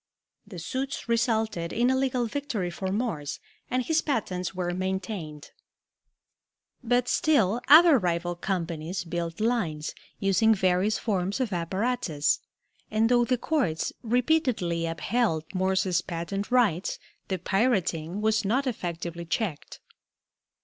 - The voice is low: No, high, 195 Hz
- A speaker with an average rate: No, slow, 120 wpm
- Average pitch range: No, wide, 5.9 semitones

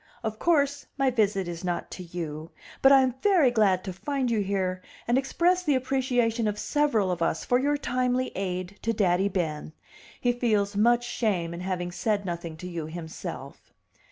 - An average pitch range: No, wide, 6.0 semitones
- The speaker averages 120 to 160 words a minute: No, average, 185 wpm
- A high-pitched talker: Yes, high, 210 Hz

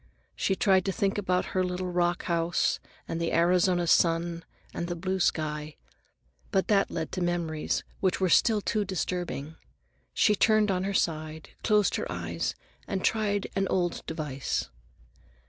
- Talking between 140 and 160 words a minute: Yes, average, 155 wpm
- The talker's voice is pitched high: No, medium, 180 Hz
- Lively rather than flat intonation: No, narrow, 2.5 semitones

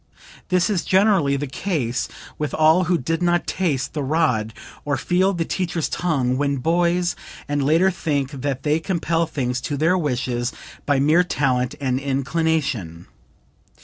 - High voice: No, medium, 150 Hz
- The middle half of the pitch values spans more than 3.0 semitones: Yes, average, 4.4 semitones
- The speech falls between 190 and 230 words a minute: No, average, 155 wpm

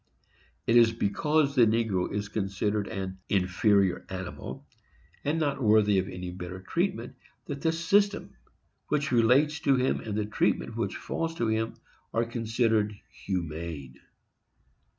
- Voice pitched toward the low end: Yes, low, 110 Hz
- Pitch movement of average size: No, wide, 5.7 semitones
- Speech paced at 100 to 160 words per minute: Yes, slow, 135 wpm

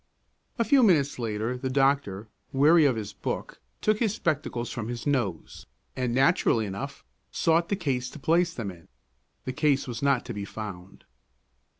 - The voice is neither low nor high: No, low, 130 Hz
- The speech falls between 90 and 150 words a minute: No, average, 170 wpm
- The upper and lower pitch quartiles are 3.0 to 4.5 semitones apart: No, wide, 5.4 semitones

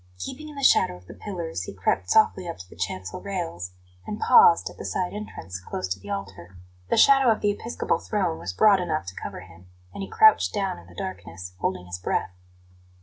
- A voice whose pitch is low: Yes, low, 100 Hz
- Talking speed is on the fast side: Yes, fast, 215 wpm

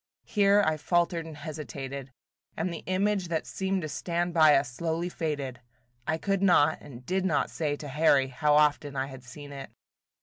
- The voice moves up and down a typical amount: Yes, average, 3.5 semitones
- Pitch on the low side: No, medium, 155 Hz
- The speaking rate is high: No, average, 180 wpm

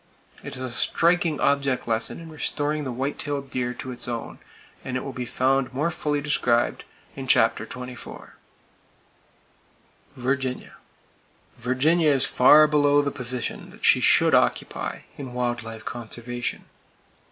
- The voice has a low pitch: Yes, low, 130 Hz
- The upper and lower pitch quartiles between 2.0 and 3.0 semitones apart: Yes, average, 2.7 semitones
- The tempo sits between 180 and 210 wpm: No, average, 140 wpm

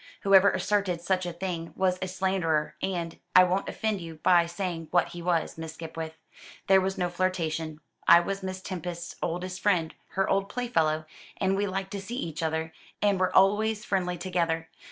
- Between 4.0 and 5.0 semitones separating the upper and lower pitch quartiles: No, narrow, 2.6 semitones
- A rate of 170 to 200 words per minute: Yes, average, 180 wpm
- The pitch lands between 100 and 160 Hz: No, medium, 180 Hz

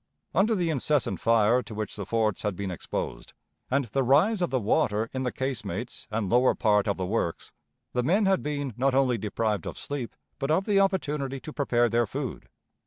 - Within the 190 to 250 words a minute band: Yes, average, 200 wpm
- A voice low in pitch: Yes, low, 125 Hz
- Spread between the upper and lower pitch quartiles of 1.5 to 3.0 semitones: No, average, 4.9 semitones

